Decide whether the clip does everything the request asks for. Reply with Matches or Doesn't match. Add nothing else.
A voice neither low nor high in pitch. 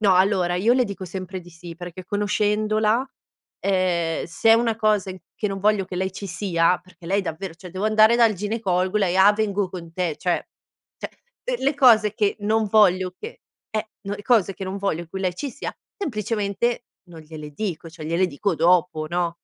Doesn't match